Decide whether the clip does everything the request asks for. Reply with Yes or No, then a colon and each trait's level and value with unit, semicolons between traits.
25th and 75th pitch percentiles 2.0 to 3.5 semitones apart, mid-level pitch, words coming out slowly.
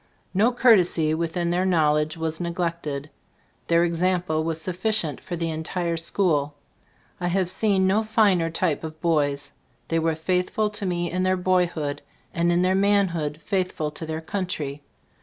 No: average, 2.8 semitones; medium, 170 Hz; average, 170 wpm